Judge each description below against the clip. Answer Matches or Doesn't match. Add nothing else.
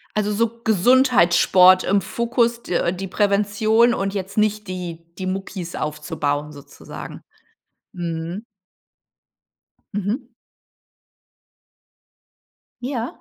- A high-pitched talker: Matches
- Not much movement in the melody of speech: Doesn't match